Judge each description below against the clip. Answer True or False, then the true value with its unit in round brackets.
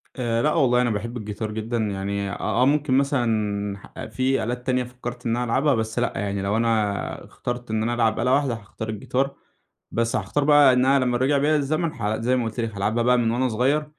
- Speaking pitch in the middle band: False (120 Hz)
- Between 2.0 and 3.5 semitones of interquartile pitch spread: True (2.9 semitones)